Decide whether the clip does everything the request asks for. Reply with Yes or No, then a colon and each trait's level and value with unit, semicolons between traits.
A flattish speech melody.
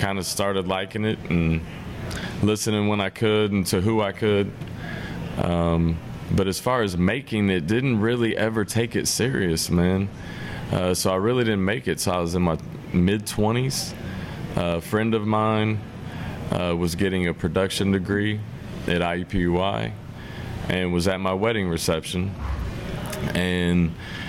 No: average, 3.3 semitones